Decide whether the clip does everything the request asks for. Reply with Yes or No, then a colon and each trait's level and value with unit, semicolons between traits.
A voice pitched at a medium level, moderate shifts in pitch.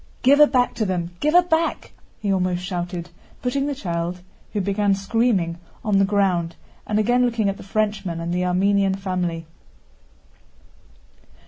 No: high, 195 Hz; average, 4.1 semitones